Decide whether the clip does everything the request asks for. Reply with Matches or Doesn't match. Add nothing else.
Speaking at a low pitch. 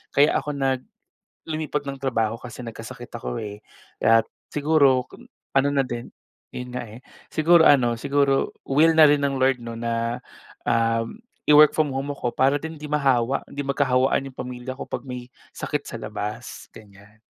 Matches